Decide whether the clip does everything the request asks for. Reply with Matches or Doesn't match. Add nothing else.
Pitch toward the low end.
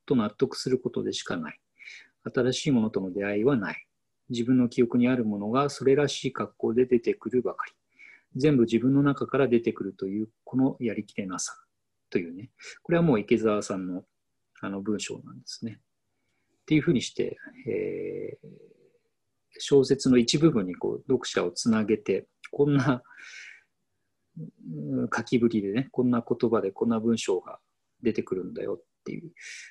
Matches